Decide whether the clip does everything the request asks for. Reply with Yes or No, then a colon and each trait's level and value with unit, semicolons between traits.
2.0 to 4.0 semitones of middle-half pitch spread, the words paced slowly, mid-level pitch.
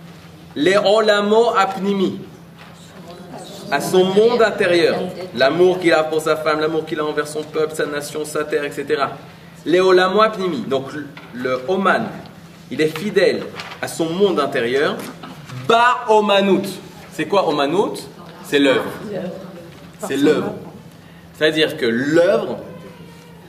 Yes: average, 3.7 semitones; slow, 120 wpm; medium, 175 Hz